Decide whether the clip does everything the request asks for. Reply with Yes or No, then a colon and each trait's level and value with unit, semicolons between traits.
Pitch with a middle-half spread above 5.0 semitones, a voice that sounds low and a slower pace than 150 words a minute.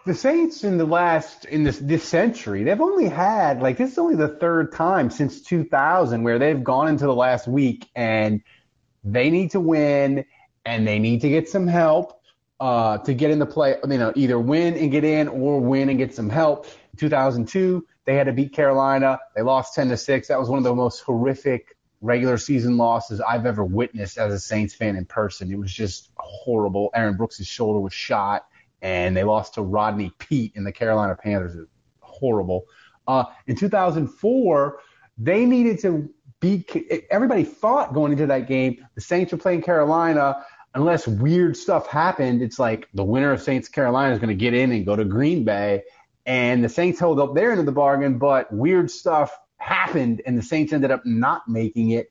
No: wide, 5.5 semitones; low, 130 Hz; average, 200 wpm